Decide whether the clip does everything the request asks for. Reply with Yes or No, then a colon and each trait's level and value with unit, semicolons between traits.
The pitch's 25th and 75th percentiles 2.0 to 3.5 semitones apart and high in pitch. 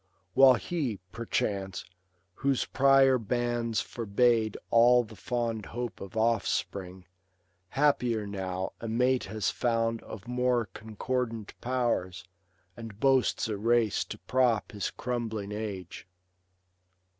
No: average, 2.9 semitones; low, 115 Hz